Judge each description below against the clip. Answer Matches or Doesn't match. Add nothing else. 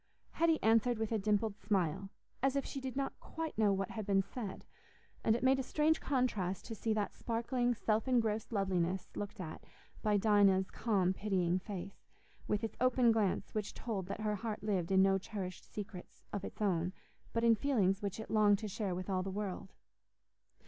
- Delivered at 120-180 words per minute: Doesn't match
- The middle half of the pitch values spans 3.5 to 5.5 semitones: Doesn't match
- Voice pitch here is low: Doesn't match